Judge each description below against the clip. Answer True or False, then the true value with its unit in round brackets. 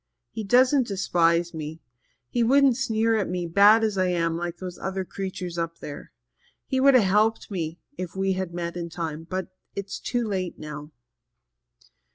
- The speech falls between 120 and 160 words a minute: False (170 wpm)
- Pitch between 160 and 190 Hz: True (185 Hz)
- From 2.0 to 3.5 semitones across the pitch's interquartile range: False (4.4 semitones)